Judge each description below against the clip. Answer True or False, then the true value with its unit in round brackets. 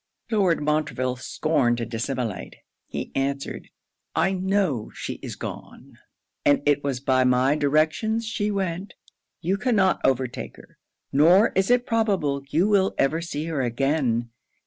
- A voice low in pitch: False (150 Hz)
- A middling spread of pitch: False (6.4 semitones)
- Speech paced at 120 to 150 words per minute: True (140 wpm)